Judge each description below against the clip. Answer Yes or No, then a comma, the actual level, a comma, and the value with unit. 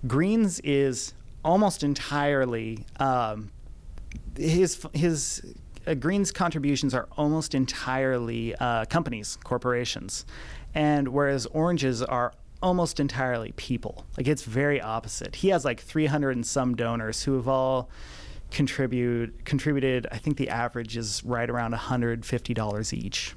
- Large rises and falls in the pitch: No, average, 3.9 semitones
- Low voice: Yes, low, 130 Hz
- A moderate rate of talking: No, slow, 125 wpm